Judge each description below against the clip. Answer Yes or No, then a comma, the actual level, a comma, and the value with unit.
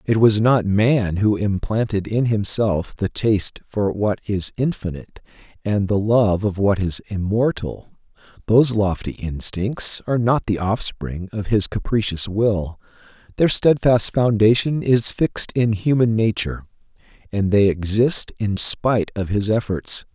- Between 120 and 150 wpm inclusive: Yes, average, 145 wpm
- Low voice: Yes, low, 105 Hz